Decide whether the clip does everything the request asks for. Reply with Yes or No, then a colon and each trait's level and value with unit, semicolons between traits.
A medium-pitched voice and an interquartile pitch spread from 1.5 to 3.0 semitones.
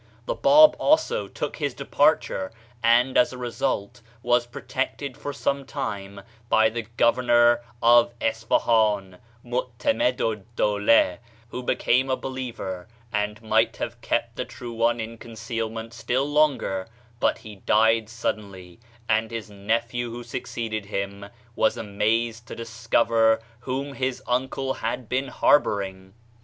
No: low, 115 Hz; average, 2.7 semitones